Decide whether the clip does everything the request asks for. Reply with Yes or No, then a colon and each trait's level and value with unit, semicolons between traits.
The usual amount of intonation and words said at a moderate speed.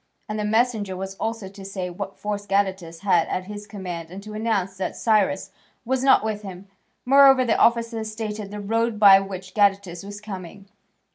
No: narrow, 2.3 semitones; average, 185 wpm